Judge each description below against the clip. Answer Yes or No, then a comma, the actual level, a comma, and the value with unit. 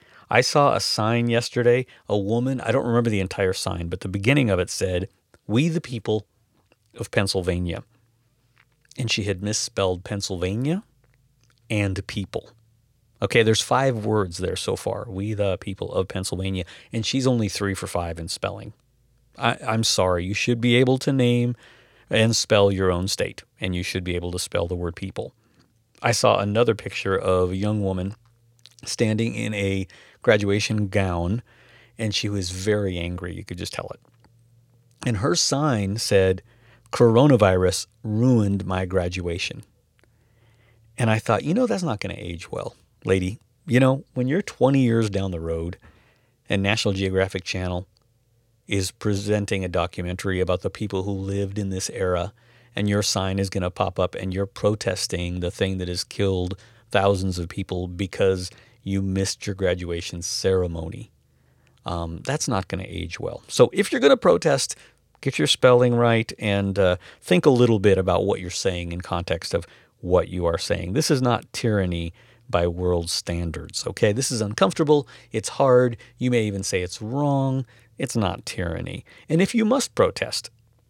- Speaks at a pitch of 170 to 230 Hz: No, low, 105 Hz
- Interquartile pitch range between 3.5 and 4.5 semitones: Yes, average, 4.1 semitones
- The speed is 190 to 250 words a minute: No, average, 170 wpm